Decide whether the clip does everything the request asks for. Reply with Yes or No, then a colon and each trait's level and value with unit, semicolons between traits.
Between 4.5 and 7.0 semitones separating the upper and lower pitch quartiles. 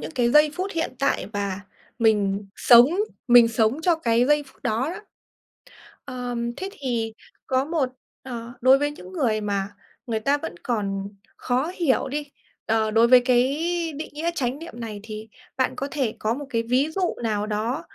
Yes: average, 4.8 semitones